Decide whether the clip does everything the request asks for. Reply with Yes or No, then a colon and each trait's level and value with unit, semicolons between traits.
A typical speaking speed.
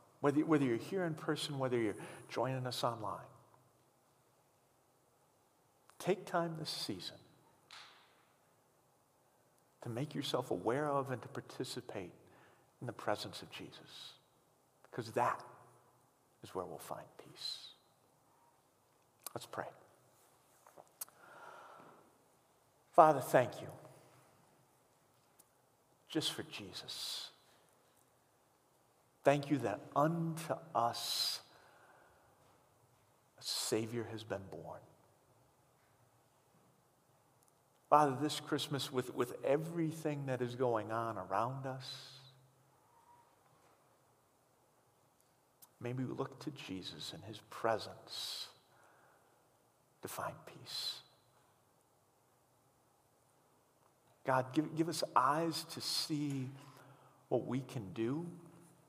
No: slow, 90 wpm